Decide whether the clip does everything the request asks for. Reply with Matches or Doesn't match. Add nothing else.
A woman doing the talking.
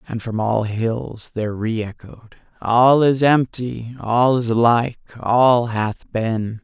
Doesn't match